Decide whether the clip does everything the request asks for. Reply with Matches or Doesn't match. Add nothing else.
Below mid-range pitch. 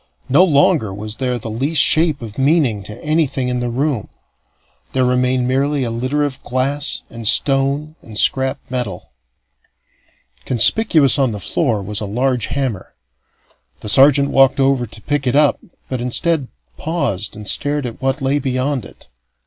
Matches